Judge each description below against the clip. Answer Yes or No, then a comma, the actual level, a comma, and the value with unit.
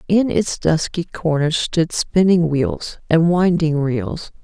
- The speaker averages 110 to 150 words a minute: Yes, slow, 135 wpm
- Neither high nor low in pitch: Yes, medium, 160 Hz